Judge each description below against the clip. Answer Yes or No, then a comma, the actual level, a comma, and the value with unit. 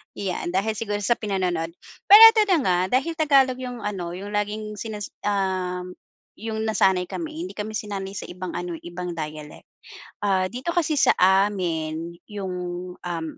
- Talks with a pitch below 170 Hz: No, high, 200 Hz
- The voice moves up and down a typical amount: Yes, average, 3.5 semitones